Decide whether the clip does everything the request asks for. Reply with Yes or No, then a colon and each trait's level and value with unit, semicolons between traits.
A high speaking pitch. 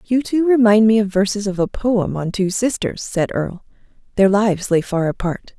Yes: high, 205 Hz